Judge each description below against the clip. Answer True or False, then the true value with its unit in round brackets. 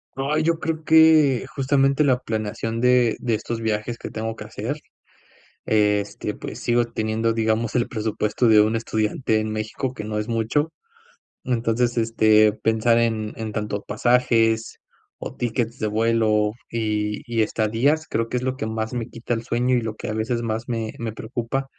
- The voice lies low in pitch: True (115 Hz)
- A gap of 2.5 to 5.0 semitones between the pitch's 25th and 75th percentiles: False (2.1 semitones)